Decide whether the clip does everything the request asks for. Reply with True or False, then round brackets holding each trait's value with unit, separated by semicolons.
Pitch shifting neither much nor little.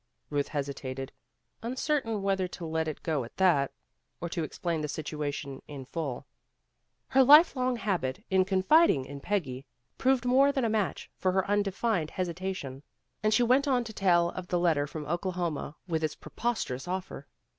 False (6.5 semitones)